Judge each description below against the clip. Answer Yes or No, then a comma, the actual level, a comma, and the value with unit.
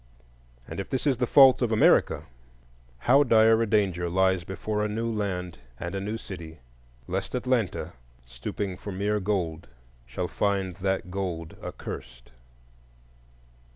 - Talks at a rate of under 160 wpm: Yes, average, 140 wpm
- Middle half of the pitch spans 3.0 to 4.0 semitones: Yes, average, 3.6 semitones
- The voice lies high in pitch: No, low, 100 Hz